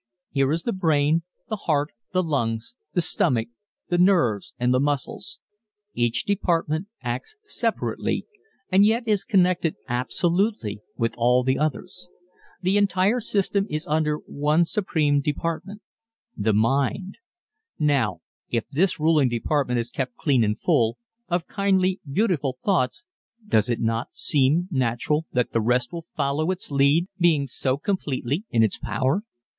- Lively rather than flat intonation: Yes, wide, 6.4 semitones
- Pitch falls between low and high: Yes, medium, 150 Hz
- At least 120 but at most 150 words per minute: Yes, average, 140 wpm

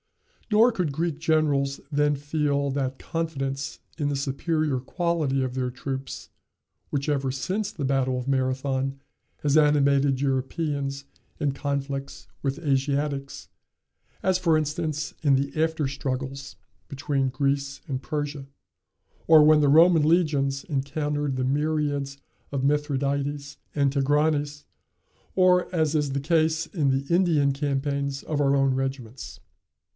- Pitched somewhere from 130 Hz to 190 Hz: Yes, medium, 140 Hz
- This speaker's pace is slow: Yes, slow, 130 wpm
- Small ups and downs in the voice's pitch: Yes, narrow, 2.1 semitones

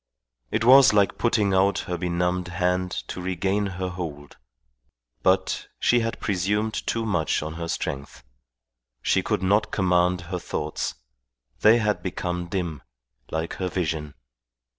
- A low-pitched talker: Yes, very low, 90 Hz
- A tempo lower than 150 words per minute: Yes, average, 140 wpm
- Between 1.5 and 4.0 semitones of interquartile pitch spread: Yes, average, 2.7 semitones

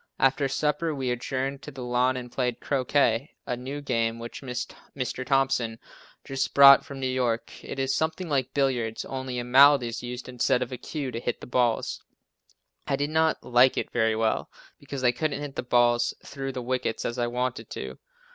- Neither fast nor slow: Yes, average, 195 wpm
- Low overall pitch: Yes, low, 130 Hz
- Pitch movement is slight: Yes, narrow, 2.1 semitones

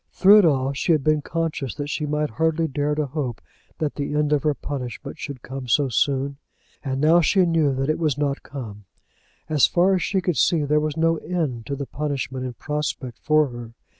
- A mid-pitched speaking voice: Yes, medium, 145 Hz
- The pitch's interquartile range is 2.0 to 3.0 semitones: Yes, narrow, 2.6 semitones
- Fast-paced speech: Yes, fast, 220 wpm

